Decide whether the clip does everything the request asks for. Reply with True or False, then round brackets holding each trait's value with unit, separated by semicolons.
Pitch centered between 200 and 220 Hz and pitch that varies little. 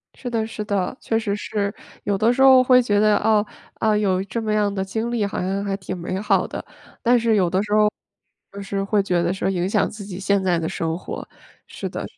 True (205 Hz; 2.3 semitones)